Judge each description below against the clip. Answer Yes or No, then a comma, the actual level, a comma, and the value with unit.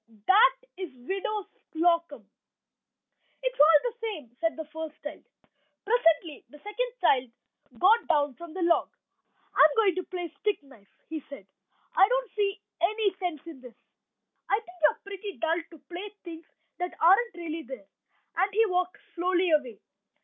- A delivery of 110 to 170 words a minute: Yes, average, 165 wpm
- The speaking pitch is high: Yes, very high, 345 Hz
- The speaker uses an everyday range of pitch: Yes, average, 4.5 semitones